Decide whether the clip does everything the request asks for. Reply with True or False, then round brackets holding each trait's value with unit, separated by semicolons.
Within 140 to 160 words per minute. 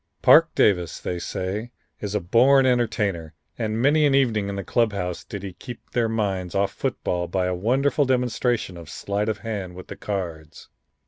False (185 wpm)